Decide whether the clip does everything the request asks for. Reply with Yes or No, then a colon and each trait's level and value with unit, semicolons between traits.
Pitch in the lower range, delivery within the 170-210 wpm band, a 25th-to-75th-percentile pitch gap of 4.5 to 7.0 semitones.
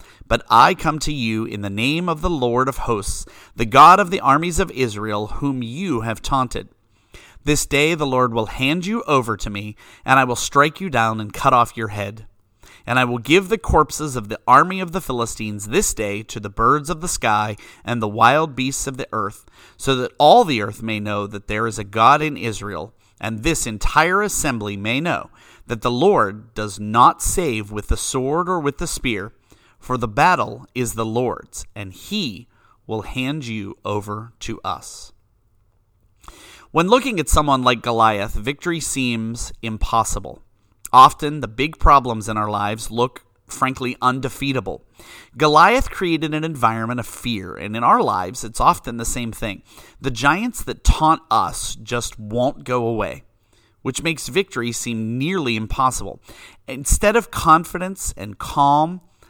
Yes: low, 120 Hz; average, 175 wpm; average, 5.0 semitones